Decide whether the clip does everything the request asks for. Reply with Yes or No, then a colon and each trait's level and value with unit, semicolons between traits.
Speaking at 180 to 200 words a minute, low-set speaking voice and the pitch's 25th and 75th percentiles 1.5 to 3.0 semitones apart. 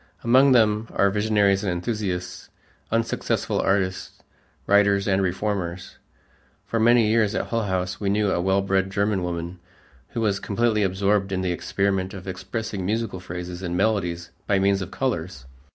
No: average, 155 wpm; low, 100 Hz; narrow, 2.5 semitones